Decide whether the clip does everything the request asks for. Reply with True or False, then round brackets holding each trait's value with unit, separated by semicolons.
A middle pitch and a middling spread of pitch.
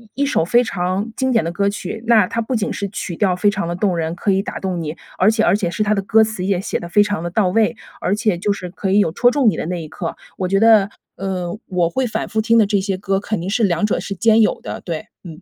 False (200 Hz; 3.3 semitones)